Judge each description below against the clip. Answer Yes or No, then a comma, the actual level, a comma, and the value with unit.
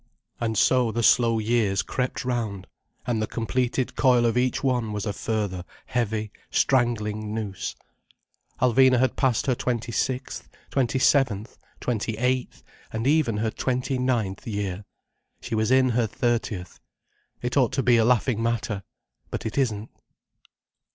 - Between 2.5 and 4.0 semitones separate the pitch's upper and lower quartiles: Yes, average, 2.8 semitones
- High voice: No, low, 115 Hz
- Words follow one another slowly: No, average, 145 wpm